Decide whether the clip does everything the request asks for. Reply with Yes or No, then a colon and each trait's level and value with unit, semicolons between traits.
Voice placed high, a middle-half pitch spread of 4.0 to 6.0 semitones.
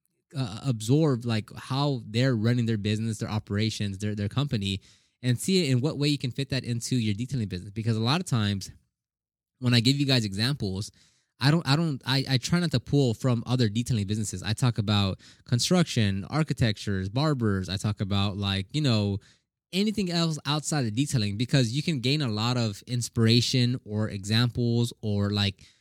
No: low, 120 Hz; average, 4.3 semitones